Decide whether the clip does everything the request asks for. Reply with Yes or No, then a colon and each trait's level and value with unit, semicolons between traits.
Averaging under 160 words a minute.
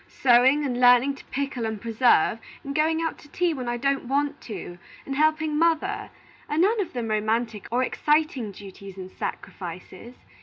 No: average, 175 wpm